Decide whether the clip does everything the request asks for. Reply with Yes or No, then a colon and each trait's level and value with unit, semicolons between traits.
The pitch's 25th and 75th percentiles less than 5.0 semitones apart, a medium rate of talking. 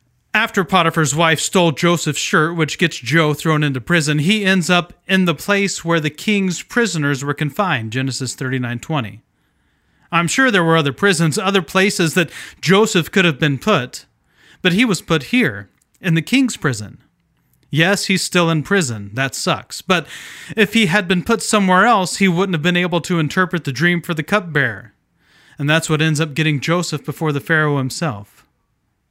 Yes: average, 4.1 semitones; average, 180 wpm